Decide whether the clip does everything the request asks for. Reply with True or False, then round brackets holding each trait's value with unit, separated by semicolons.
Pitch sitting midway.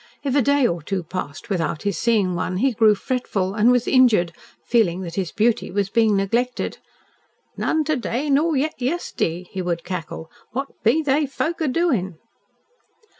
False (225 Hz)